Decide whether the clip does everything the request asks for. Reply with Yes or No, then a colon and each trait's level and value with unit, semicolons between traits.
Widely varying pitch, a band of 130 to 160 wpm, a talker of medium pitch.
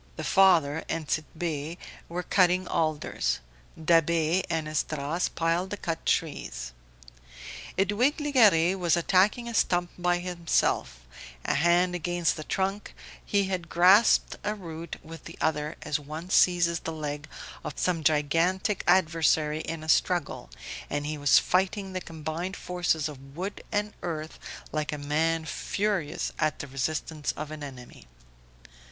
No: average, 2.9 semitones; average, 140 wpm; medium, 165 Hz